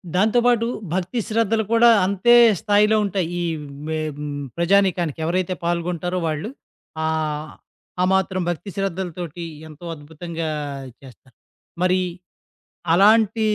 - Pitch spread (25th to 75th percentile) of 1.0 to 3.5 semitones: No, average, 4.1 semitones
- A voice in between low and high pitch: Yes, medium, 180 Hz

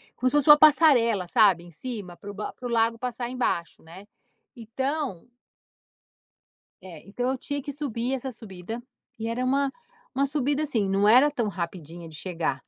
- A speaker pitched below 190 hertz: No, high, 230 Hz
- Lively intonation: Yes, wide, 5.8 semitones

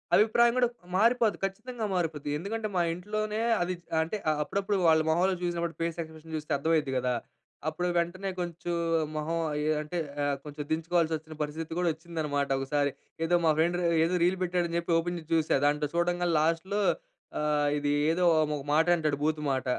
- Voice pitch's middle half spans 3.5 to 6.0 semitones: No, average, 2.8 semitones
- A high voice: No, medium, 165 Hz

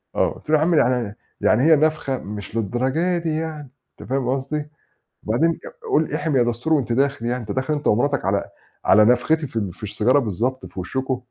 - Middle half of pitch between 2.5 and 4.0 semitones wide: No, average, 4.9 semitones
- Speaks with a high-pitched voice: No, low, 130 Hz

